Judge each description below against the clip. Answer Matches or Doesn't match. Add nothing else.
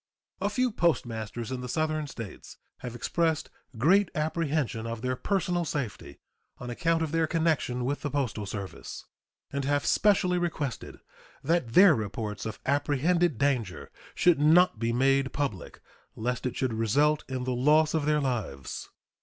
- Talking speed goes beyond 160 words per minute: Doesn't match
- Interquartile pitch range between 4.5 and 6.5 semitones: Matches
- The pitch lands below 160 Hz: Matches